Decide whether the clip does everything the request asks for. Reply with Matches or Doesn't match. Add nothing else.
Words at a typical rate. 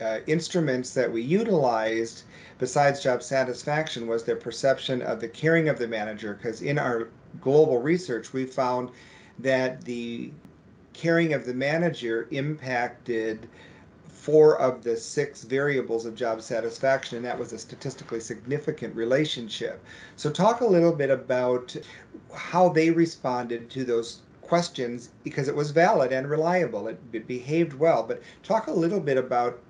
Matches